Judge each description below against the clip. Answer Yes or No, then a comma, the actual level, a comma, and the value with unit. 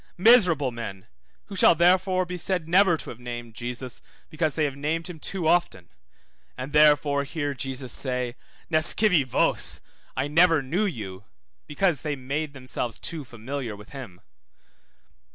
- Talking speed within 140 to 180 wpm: Yes, average, 150 wpm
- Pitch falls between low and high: Yes, medium, 145 Hz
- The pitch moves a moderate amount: Yes, average, 5.0 semitones